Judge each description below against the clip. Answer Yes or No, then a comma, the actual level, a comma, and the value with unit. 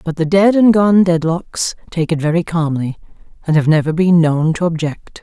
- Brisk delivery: No, average, 195 wpm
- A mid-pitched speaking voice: Yes, medium, 165 Hz